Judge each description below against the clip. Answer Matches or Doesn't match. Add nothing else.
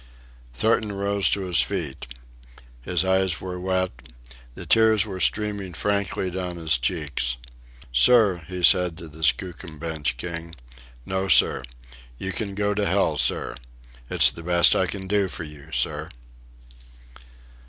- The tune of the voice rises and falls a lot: Doesn't match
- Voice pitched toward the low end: Matches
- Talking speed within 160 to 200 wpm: Doesn't match